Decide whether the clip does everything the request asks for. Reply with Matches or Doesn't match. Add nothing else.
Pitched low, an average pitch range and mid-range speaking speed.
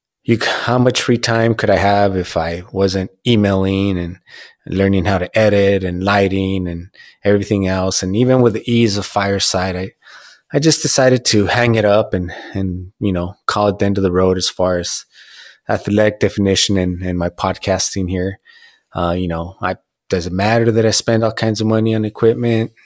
Matches